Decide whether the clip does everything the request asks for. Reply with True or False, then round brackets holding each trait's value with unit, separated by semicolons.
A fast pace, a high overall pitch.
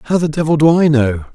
False (270 wpm; 150 Hz)